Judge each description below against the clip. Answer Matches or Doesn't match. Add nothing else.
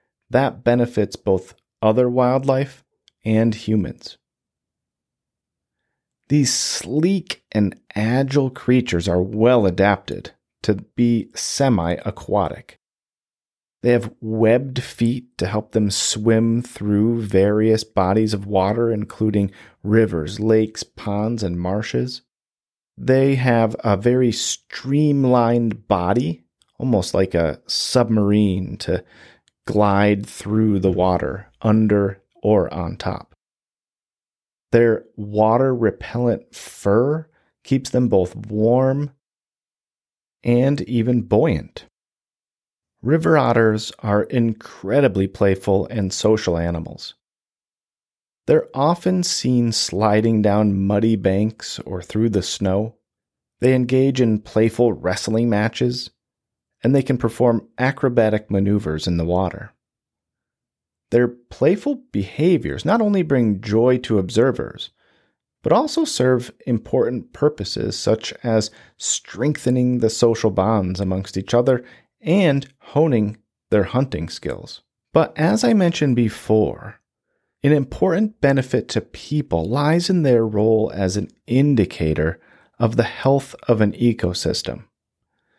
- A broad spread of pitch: Doesn't match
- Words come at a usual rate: Doesn't match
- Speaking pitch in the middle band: Doesn't match